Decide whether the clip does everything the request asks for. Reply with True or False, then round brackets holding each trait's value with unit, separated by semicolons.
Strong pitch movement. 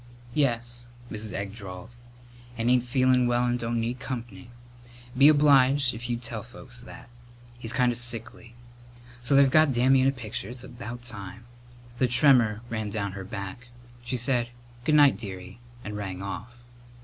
False (2.6 semitones)